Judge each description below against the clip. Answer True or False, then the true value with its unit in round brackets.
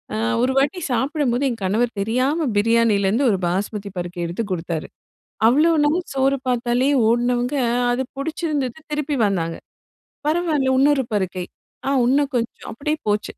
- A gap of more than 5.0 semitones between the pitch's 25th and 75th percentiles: True (5.4 semitones)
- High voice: True (245 Hz)